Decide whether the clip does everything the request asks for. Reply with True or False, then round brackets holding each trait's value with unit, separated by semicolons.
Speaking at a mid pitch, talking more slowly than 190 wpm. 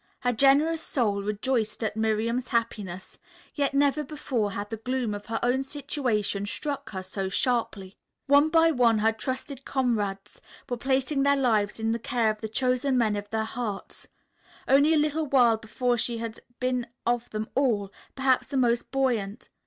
False (240 Hz; 170 wpm)